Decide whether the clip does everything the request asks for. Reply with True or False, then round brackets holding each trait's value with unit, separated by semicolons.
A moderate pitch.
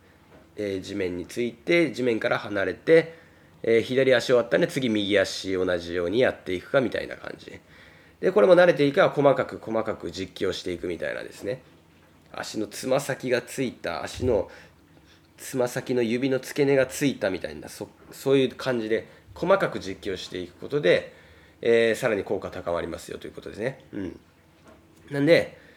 False (115 Hz)